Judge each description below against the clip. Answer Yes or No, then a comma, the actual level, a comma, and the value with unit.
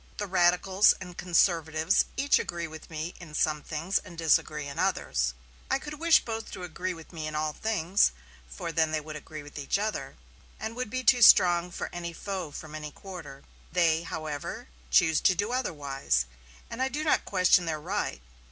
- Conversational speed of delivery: Yes, average, 190 wpm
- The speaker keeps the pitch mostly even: No, average, 4.0 semitones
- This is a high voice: No, medium, 170 Hz